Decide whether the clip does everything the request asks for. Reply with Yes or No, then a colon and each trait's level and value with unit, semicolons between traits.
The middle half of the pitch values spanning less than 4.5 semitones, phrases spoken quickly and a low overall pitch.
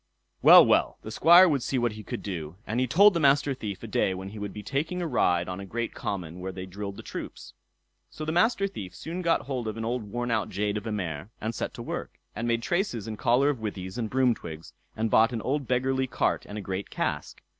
No: average, 5.2 semitones; fast, 250 wpm; low, 115 Hz